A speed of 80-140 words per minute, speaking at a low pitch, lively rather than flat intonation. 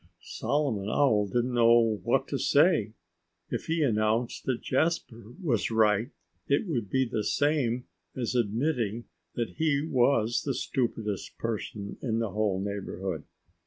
No: slow, 135 wpm; low, 115 Hz; average, 4.1 semitones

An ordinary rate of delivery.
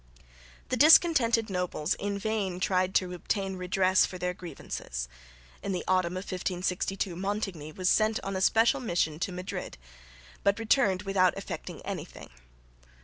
Yes: average, 145 wpm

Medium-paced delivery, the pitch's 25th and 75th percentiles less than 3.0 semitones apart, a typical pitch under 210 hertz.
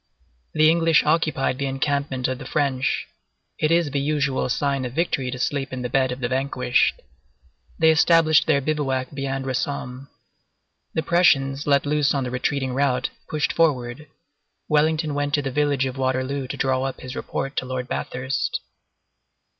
Yes: average, 165 wpm; narrow, 2.4 semitones; medium, 140 Hz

